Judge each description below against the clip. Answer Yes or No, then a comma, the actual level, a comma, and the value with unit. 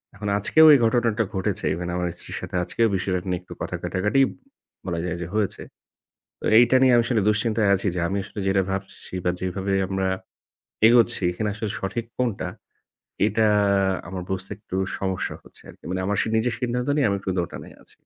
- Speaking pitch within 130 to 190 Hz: No, low, 100 Hz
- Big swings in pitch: No, average, 3.6 semitones